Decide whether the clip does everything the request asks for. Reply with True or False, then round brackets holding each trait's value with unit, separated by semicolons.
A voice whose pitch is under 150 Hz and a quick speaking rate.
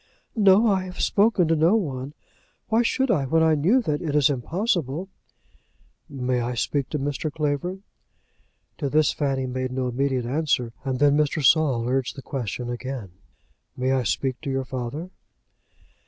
False (140 Hz; 165 wpm)